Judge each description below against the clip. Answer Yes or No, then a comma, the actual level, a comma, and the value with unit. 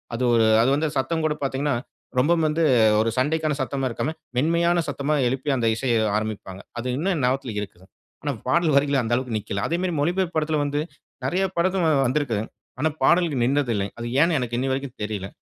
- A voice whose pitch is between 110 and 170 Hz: Yes, medium, 140 Hz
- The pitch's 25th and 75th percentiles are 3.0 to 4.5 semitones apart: No, average, 4.9 semitones